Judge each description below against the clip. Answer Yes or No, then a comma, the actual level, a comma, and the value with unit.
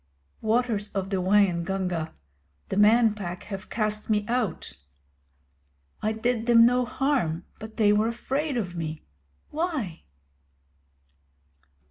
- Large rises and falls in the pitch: No, average, 3.9 semitones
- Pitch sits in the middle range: No, high, 215 Hz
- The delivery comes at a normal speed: No, slow, 115 wpm